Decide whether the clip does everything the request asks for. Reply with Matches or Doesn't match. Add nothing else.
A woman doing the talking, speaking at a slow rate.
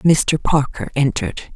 Matches